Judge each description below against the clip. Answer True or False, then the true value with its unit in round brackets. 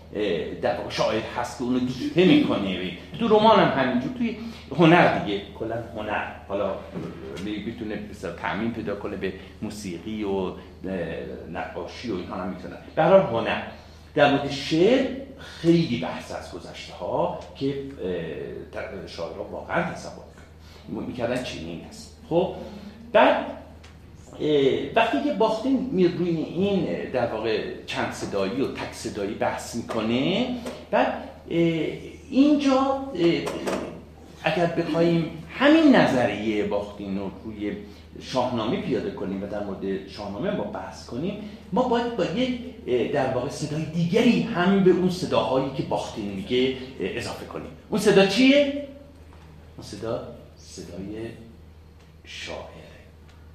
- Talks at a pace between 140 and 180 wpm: False (120 wpm)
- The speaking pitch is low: True (120 Hz)